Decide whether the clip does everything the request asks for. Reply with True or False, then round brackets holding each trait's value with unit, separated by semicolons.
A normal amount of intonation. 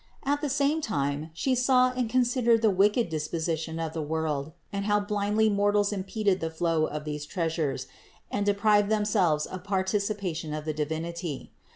True (5.0 semitones)